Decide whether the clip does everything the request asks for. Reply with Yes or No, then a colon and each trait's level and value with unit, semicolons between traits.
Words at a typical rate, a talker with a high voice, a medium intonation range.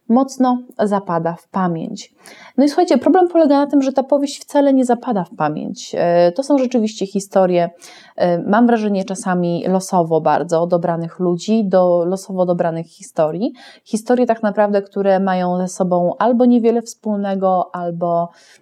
No: average, 145 wpm; high, 195 Hz; wide, 5.7 semitones